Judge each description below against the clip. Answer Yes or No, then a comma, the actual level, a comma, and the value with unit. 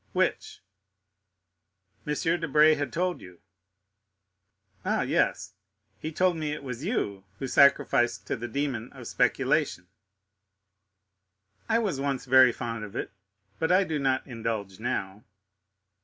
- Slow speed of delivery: Yes, slow, 125 wpm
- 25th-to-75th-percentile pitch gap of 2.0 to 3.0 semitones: No, average, 4.9 semitones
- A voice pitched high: No, low, 135 Hz